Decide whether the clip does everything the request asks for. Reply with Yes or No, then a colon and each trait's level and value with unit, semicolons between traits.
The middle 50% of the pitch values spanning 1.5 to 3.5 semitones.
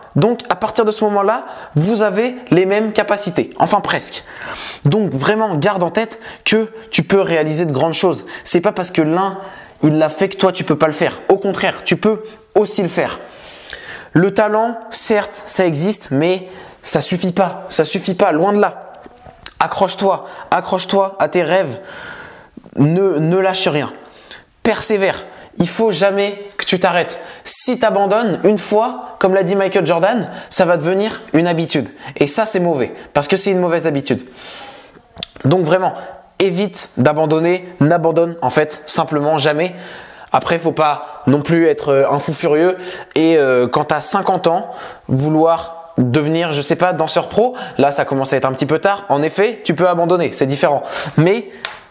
No: average, 4.2 semitones